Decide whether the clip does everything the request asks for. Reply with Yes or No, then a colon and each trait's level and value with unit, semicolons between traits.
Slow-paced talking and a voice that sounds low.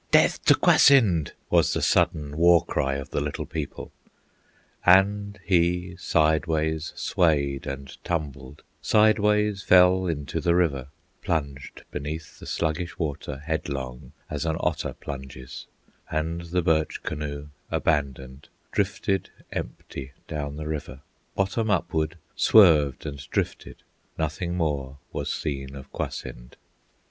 Yes: slow, 120 wpm; very low, 80 Hz